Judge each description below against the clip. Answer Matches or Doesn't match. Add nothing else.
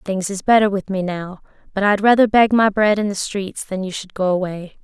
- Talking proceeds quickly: Matches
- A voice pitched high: Matches